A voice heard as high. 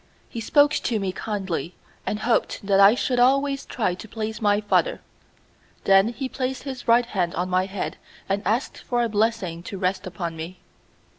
Yes: high, 210 Hz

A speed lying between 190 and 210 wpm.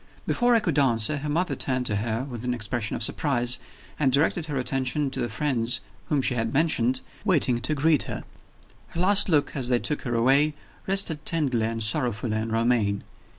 Yes: average, 195 wpm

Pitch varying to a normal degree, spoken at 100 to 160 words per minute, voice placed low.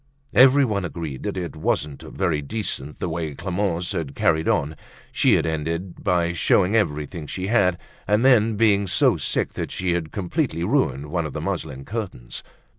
No: average, 4.8 semitones; average, 170 wpm; very low, 85 Hz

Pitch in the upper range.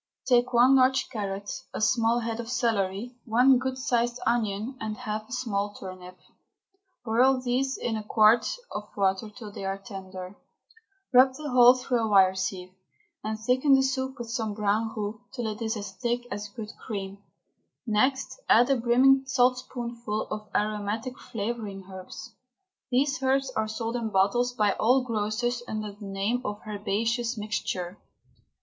Yes: high, 225 Hz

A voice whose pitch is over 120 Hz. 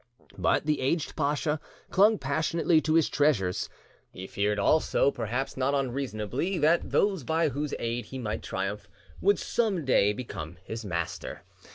Yes: low, 135 Hz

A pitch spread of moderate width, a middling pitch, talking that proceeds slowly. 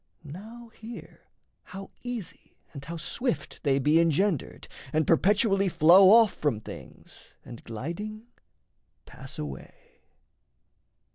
No: wide, 6.2 semitones; medium, 175 Hz; slow, 110 wpm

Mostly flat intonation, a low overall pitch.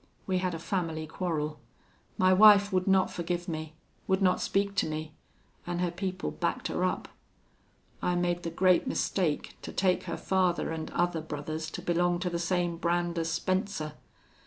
No: narrow, 2.3 semitones; medium, 175 Hz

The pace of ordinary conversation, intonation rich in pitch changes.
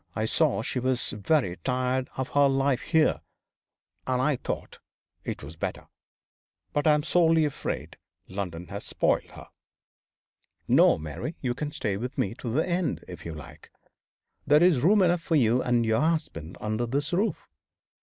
Yes: average, 165 wpm; wide, 6.0 semitones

